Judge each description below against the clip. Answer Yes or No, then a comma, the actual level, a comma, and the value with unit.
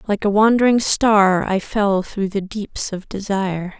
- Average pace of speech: Yes, average, 175 wpm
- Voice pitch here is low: No, high, 200 Hz